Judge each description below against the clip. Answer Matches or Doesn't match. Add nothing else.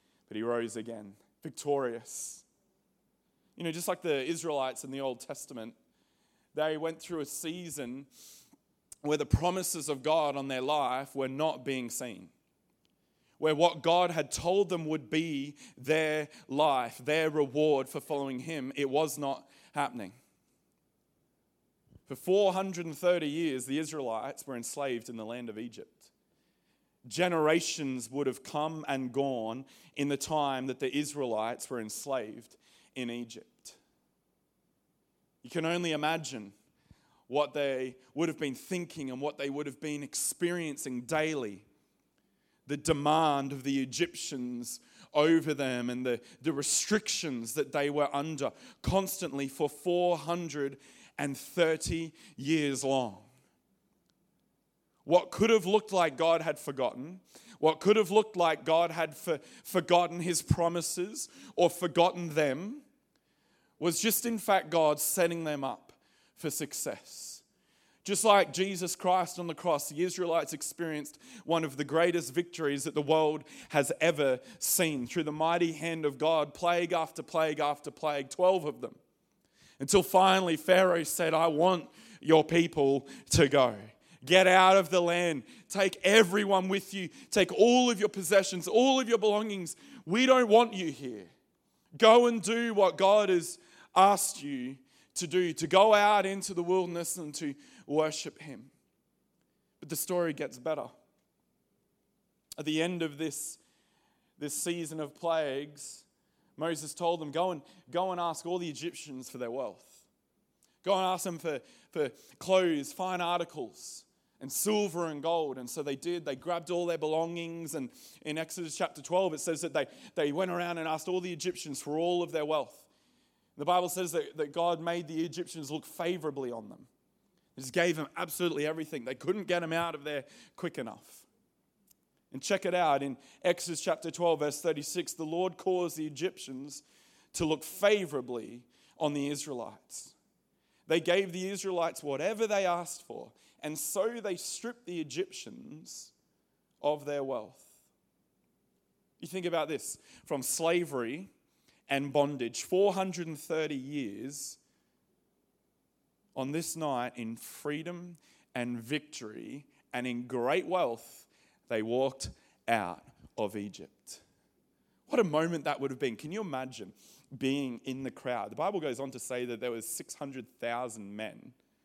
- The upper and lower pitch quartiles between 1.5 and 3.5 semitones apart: Doesn't match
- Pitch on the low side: Doesn't match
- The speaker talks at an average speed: Matches